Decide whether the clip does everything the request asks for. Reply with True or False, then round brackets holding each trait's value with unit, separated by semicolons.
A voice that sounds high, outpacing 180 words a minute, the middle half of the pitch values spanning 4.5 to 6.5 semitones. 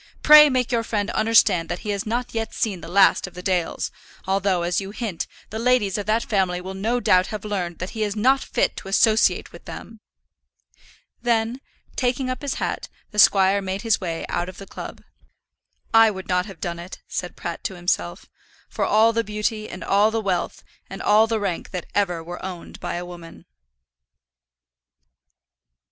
False (200 Hz; 190 wpm; 3.7 semitones)